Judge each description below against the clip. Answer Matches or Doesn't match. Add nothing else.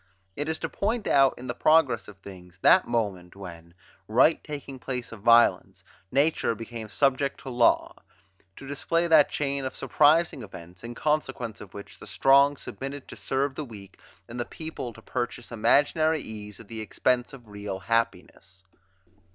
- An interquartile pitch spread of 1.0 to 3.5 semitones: Doesn't match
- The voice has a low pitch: Matches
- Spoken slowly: Doesn't match